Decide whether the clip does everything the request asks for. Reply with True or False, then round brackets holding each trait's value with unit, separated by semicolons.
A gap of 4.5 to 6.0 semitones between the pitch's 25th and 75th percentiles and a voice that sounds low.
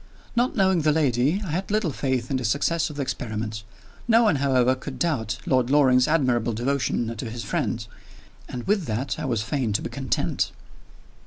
True (4.9 semitones; 130 Hz)